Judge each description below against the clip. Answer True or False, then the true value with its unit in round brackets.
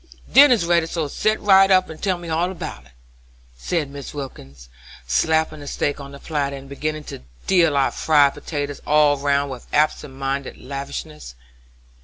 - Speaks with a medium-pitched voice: True (145 Hz)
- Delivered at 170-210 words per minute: True (175 wpm)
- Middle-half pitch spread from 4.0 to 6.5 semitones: False (3.0 semitones)